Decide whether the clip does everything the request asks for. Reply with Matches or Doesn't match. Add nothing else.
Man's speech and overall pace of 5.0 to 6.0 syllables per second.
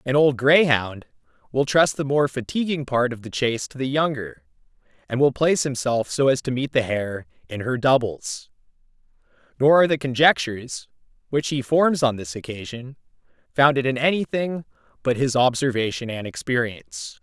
Matches